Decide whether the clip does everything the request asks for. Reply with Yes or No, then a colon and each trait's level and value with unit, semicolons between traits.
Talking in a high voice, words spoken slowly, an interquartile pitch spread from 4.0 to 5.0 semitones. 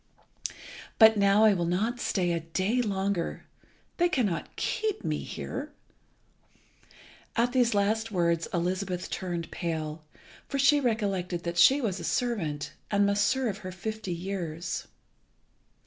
Yes: high, 195 Hz; slow, 130 wpm; average, 4.4 semitones